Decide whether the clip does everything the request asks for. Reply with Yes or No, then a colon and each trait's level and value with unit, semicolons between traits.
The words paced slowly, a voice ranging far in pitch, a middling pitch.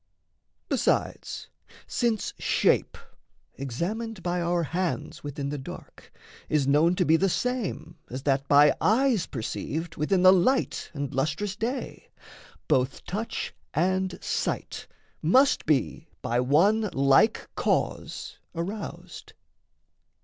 Yes: slow, 115 wpm; wide, 6.0 semitones; medium, 170 Hz